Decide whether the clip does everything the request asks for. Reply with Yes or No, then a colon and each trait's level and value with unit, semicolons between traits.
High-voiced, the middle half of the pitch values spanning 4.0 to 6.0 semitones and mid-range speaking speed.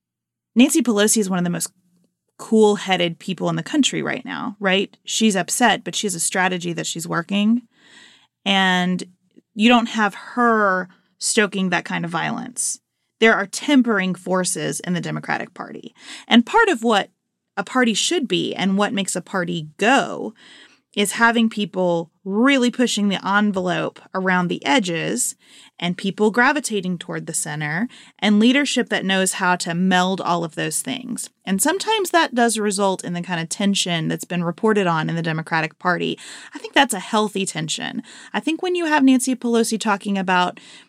Yes: high, 200 Hz; average, 4.8 semitones; average, 175 wpm